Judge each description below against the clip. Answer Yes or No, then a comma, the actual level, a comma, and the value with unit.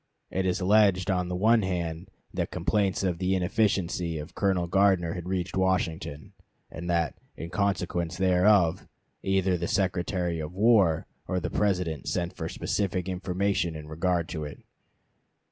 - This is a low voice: Yes, very low, 90 Hz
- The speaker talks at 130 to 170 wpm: Yes, average, 150 wpm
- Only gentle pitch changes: Yes, narrow, 2.2 semitones